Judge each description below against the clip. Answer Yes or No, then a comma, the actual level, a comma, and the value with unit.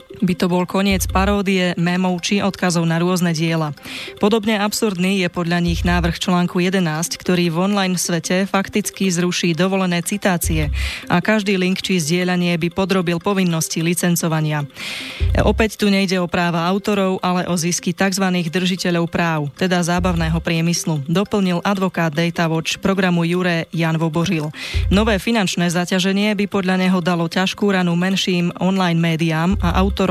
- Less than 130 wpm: No, average, 145 wpm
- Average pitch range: No, narrow, 2.1 semitones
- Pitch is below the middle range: No, medium, 180 Hz